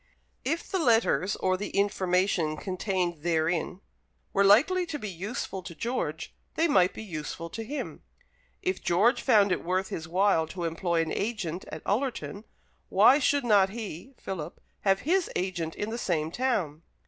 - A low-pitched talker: No, high, 195 Hz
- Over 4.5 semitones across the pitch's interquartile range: Yes, average, 5.2 semitones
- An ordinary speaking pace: Yes, average, 160 wpm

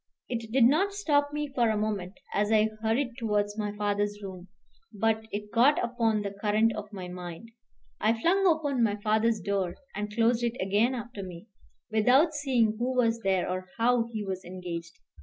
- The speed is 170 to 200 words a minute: Yes, average, 180 wpm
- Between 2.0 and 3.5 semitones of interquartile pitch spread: Yes, average, 2.9 semitones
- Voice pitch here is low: No, high, 220 Hz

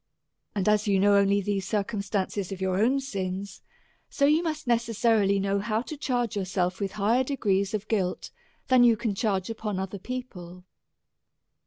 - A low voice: No, high, 205 Hz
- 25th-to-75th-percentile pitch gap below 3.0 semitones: No, average, 3.3 semitones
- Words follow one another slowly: No, average, 170 wpm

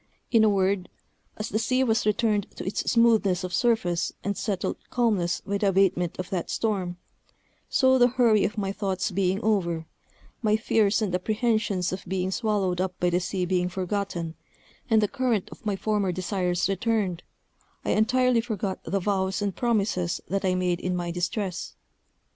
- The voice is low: No, high, 195 Hz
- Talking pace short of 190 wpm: Yes, average, 170 wpm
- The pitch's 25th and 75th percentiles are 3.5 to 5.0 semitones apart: No, average, 3.1 semitones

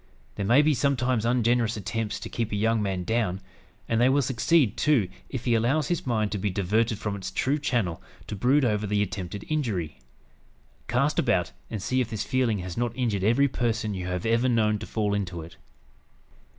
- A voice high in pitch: No, low, 115 Hz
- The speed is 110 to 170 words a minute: No, average, 200 wpm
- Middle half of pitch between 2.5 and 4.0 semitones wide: Yes, average, 3.5 semitones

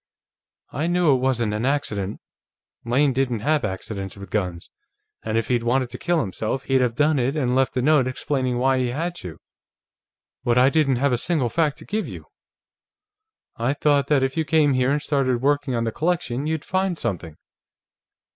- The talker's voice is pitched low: Yes, low, 130 Hz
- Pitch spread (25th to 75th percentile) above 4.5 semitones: No, average, 3.7 semitones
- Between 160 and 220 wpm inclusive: Yes, average, 190 wpm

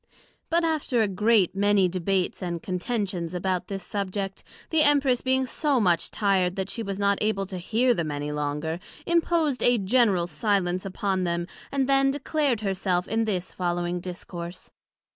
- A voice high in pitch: Yes, high, 195 Hz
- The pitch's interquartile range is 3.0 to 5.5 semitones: Yes, average, 5.2 semitones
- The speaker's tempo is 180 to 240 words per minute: No, average, 165 wpm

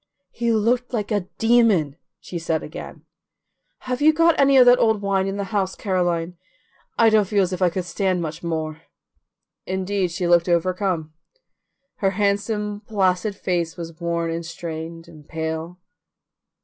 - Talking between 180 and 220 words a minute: No, average, 160 wpm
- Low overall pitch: No, medium, 185 Hz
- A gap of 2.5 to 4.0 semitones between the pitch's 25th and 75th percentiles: Yes, average, 3.7 semitones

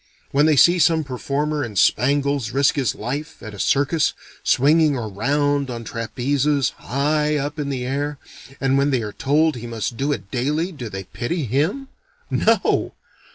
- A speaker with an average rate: Yes, average, 165 wpm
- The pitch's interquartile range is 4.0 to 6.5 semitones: No, average, 3.4 semitones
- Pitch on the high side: No, medium, 140 Hz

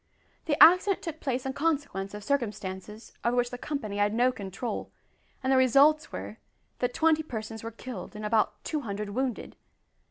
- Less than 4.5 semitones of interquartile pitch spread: No, average, 5.1 semitones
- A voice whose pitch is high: Yes, high, 245 Hz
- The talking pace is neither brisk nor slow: Yes, average, 170 wpm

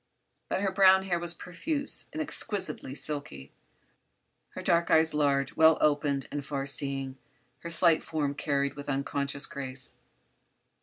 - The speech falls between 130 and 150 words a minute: Yes, average, 140 wpm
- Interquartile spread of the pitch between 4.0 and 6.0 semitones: No, average, 3.5 semitones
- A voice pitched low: No, medium, 145 Hz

